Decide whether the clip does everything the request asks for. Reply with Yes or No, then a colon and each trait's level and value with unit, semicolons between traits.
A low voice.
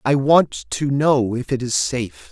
Yes: low, 130 Hz